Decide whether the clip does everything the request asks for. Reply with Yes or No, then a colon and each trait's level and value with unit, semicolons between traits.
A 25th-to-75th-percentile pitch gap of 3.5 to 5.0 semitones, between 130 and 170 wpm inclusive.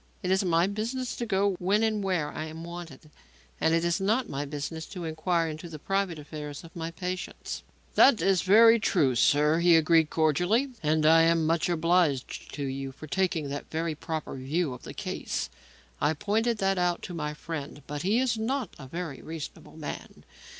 No: average, 4.0 semitones; average, 190 wpm